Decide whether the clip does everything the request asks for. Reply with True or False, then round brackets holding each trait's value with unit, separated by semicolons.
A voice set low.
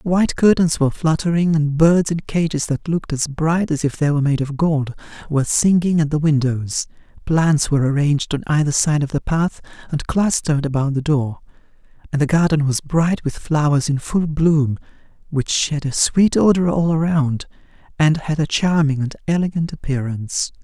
False (150 Hz)